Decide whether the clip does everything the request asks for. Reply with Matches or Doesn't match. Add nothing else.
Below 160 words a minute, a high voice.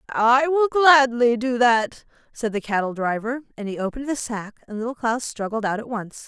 Doesn't match